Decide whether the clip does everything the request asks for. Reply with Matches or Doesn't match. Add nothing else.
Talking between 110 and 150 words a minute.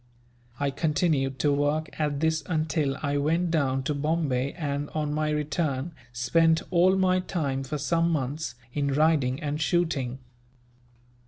Matches